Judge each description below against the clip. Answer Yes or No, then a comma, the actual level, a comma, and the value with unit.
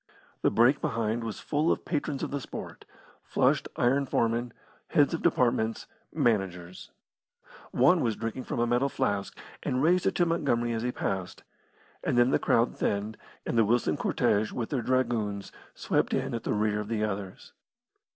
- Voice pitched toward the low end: Yes, low, 120 Hz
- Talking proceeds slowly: No, average, 170 wpm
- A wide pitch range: No, average, 3.8 semitones